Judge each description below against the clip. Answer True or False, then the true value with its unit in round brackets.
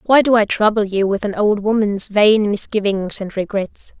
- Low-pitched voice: False (205 Hz)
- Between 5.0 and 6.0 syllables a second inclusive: False (4.6 syllables/s)